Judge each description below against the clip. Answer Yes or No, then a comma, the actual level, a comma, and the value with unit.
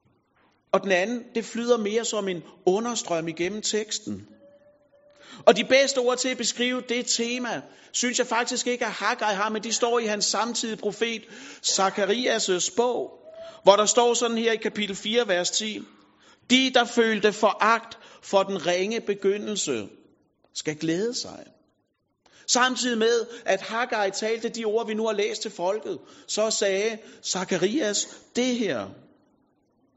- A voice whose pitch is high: Yes, high, 225 Hz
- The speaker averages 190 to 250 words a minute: No, average, 150 wpm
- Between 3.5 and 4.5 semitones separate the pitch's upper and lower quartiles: No, average, 3.0 semitones